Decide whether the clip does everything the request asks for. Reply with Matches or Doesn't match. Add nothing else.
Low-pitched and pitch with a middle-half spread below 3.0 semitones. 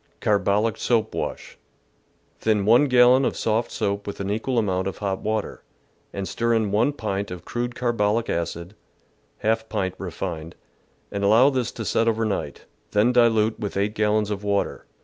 Matches